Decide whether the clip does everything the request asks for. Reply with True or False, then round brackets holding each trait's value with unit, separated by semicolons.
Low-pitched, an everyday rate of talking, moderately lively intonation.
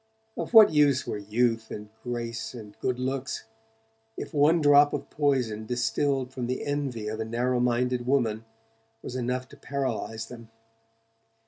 True (125 Hz; 150 wpm; 3.3 semitones)